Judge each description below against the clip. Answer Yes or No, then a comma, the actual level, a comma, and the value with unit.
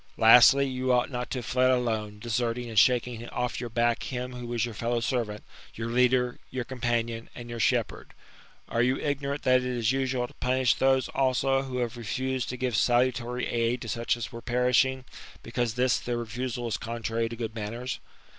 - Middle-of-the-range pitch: No, low, 120 Hz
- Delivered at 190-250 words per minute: Yes, average, 200 wpm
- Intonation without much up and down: Yes, narrow, 1.6 semitones